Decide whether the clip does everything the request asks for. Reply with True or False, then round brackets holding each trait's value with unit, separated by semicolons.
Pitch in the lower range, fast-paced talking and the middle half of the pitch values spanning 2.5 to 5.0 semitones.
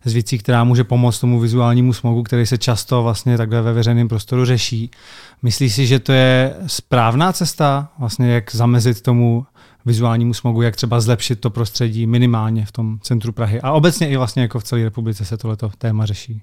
False (120 Hz; 190 wpm; 1.4 semitones)